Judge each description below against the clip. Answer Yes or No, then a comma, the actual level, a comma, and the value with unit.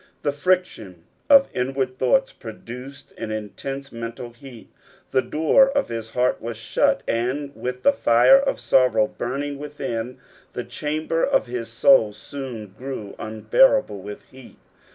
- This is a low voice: Yes, low, 125 Hz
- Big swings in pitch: No, average, 4.0 semitones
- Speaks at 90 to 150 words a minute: Yes, average, 140 wpm